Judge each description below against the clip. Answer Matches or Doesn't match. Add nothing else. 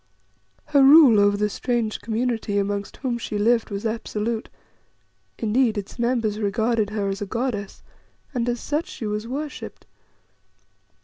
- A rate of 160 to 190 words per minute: Doesn't match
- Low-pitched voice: Doesn't match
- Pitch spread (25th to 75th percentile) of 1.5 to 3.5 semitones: Matches